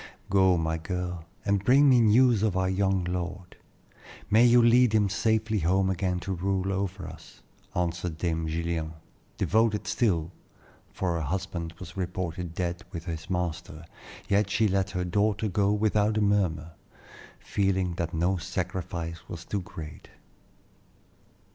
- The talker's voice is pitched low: Yes, very low, 95 Hz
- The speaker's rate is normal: Yes, average, 145 wpm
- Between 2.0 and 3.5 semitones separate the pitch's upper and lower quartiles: Yes, average, 3.1 semitones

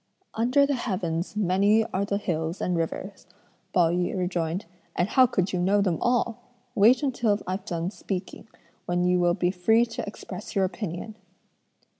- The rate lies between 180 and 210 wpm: No, average, 165 wpm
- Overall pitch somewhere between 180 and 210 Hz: Yes, high, 190 Hz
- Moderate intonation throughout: Yes, average, 3.7 semitones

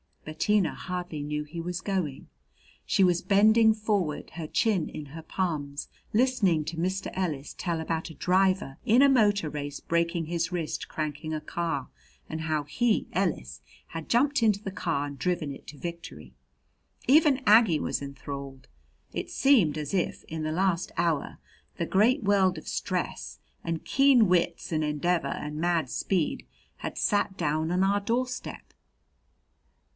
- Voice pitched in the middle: Yes, medium, 170 Hz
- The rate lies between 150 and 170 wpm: Yes, average, 160 wpm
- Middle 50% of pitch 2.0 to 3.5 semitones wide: No, average, 4.7 semitones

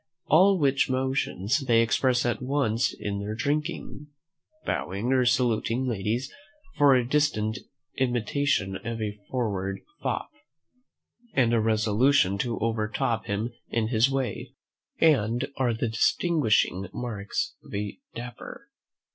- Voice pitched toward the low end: Yes, low, 120 Hz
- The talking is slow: Yes, slow, 120 wpm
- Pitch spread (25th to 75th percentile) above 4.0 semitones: No, average, 3.7 semitones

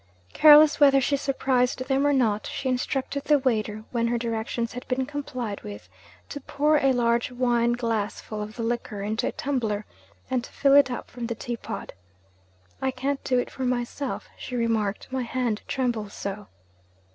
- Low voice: No, high, 245 Hz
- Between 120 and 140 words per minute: No, average, 180 wpm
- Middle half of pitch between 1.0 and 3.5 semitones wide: Yes, average, 2.8 semitones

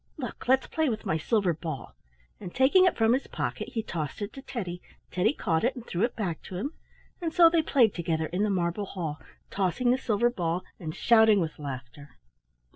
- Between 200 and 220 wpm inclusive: Yes, fast, 205 wpm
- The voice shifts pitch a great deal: Yes, wide, 6.4 semitones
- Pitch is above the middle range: Yes, high, 200 Hz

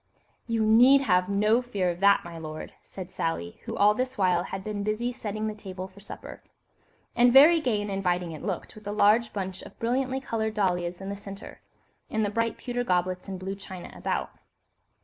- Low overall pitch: No, high, 205 Hz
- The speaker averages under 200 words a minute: No, fast, 205 wpm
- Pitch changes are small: No, average, 3.6 semitones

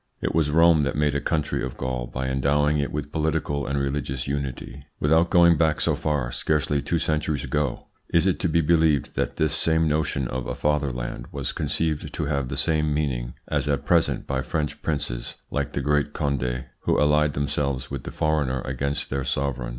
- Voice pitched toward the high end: No, very low, 75 Hz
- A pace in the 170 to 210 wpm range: Yes, average, 195 wpm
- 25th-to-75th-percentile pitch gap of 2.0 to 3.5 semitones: Yes, narrow, 2.4 semitones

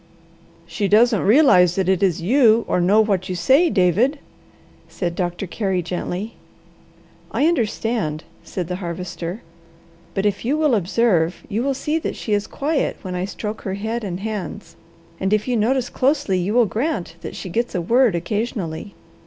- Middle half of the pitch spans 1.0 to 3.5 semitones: No, average, 4.7 semitones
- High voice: Yes, high, 205 Hz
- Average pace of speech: Yes, average, 170 wpm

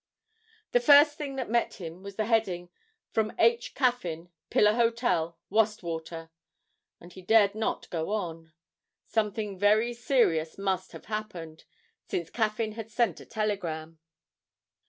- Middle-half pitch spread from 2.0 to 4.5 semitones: No, average, 4.9 semitones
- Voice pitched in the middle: No, high, 210 Hz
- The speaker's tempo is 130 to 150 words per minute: Yes, slow, 135 wpm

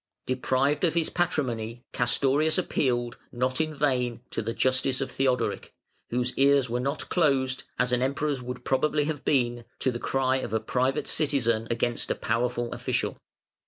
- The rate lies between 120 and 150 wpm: No, average, 160 wpm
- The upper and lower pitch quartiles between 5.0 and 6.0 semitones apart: No, narrow, 2.6 semitones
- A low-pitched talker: Yes, low, 130 Hz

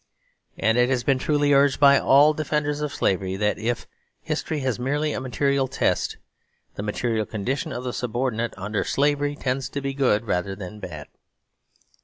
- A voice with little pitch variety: No, average, 4.6 semitones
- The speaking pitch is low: Yes, low, 130 Hz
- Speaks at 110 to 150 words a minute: No, average, 170 wpm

